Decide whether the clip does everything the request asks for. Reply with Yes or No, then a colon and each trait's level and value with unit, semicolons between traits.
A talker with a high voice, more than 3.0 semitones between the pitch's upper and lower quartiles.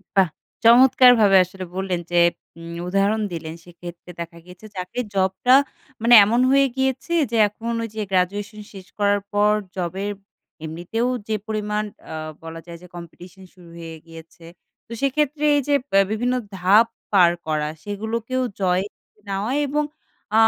Yes: high, 200 Hz; average, 4.5 semitones